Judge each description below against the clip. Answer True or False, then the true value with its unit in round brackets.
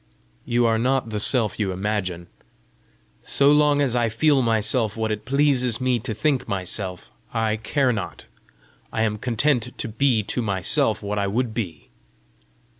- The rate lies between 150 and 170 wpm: True (160 wpm)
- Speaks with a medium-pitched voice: False (115 Hz)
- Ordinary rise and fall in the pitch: True (3.4 semitones)